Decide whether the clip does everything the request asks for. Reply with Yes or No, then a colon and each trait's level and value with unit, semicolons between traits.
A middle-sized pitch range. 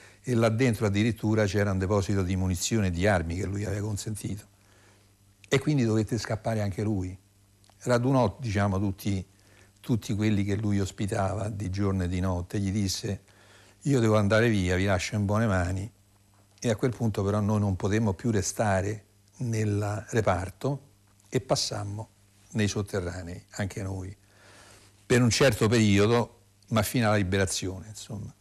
No: narrow, 1.9 semitones